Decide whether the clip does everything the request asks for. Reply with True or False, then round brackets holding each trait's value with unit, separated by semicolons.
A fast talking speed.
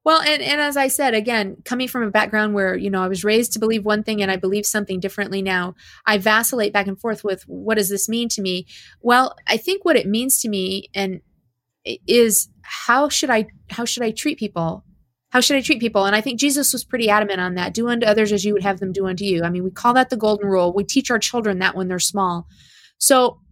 True (255 wpm)